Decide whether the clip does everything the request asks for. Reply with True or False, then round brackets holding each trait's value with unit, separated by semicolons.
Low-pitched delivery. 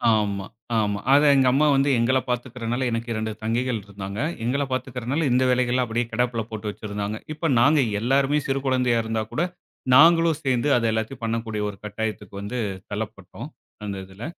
True (120 Hz)